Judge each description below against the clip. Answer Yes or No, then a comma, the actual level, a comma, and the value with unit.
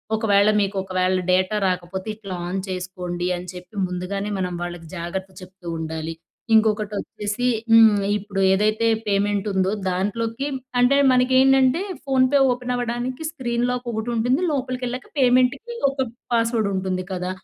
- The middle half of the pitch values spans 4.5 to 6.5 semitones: Yes, average, 5.0 semitones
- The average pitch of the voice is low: No, high, 210 Hz